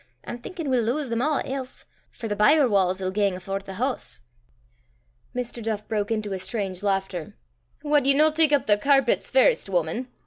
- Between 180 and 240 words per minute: Yes, average, 185 wpm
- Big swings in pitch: Yes, wide, 5.8 semitones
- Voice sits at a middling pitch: No, high, 225 Hz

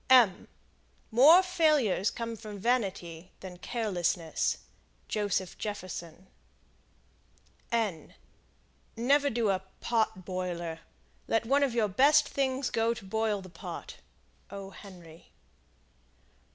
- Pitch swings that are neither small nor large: Yes, average, 4.5 semitones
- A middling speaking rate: No, slow, 100 wpm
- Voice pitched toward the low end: No, high, 210 Hz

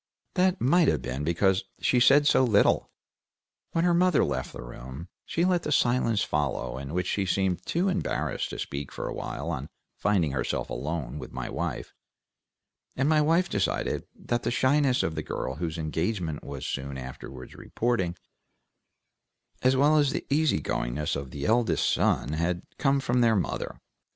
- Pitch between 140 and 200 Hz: No, very low, 95 Hz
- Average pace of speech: Yes, average, 170 wpm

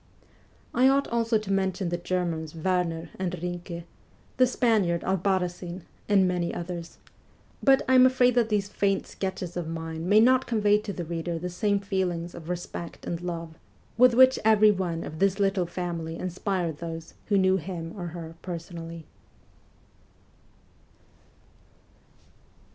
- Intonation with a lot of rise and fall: No, average, 3.2 semitones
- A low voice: No, medium, 180 Hz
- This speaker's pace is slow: No, average, 145 wpm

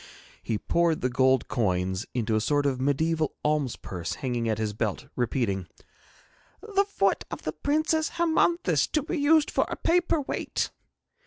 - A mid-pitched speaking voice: Yes, medium, 145 Hz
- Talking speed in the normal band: Yes, average, 160 wpm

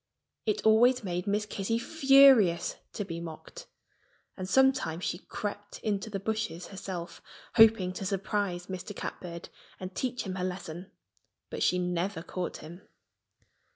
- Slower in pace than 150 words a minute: Yes, average, 140 wpm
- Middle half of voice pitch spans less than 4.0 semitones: Yes, average, 3.5 semitones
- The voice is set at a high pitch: Yes, high, 195 Hz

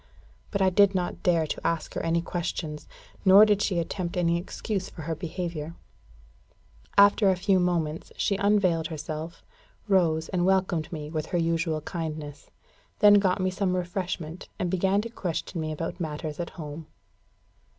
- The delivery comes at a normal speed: Yes, average, 160 wpm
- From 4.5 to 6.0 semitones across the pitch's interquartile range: No, average, 2.9 semitones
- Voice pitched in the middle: Yes, medium, 175 Hz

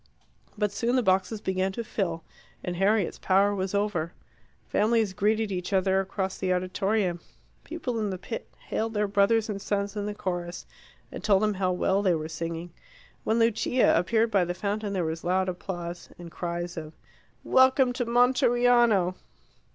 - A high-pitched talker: Yes, high, 195 Hz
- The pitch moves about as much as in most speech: Yes, average, 3.4 semitones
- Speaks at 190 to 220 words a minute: No, average, 165 wpm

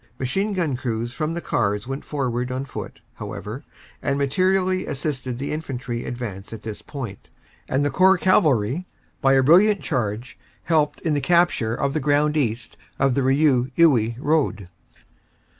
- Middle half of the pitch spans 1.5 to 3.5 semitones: No, average, 4.4 semitones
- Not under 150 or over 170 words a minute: Yes, average, 160 wpm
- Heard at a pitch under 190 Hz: Yes, low, 135 Hz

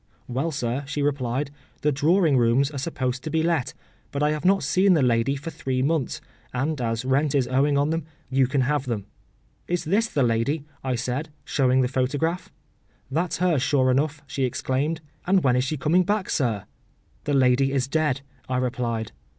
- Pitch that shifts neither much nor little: Yes, average, 3.3 semitones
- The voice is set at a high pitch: No, medium, 140 Hz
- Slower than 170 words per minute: No, average, 185 wpm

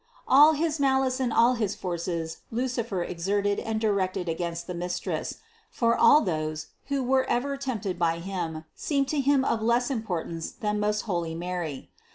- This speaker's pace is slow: No, average, 165 wpm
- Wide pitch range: Yes, wide, 6.9 semitones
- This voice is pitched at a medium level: No, high, 210 Hz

